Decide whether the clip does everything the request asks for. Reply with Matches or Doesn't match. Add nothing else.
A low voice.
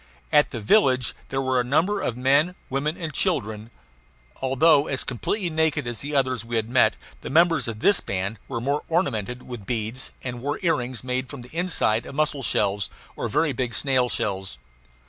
Matches